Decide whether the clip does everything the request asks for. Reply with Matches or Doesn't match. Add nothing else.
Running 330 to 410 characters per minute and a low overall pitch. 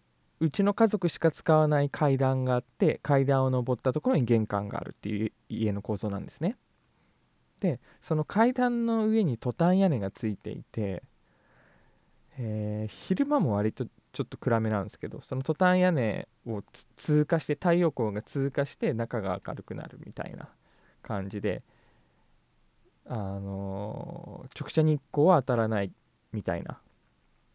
Doesn't match